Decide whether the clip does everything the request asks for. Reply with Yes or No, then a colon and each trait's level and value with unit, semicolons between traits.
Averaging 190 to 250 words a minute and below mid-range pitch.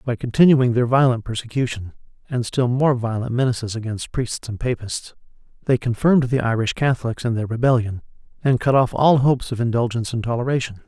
No: average, 170 wpm; low, 120 Hz